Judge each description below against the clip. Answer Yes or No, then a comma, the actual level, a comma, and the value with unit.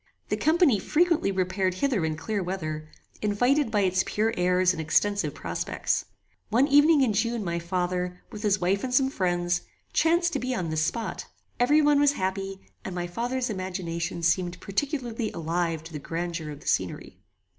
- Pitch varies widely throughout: Yes, wide, 5.8 semitones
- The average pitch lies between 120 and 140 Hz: No, high, 190 Hz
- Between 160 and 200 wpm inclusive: Yes, average, 175 wpm